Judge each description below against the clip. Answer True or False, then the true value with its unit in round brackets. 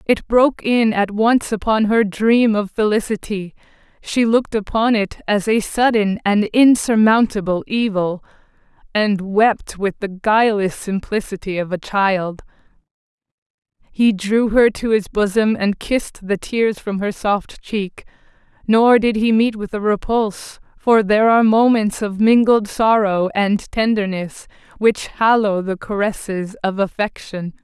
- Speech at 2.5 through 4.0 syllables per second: False (4.3 syllables/s)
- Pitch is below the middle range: False (210 Hz)